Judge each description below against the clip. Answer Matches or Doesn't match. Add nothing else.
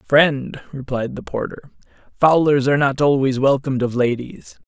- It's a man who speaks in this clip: Matches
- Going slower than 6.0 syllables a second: Matches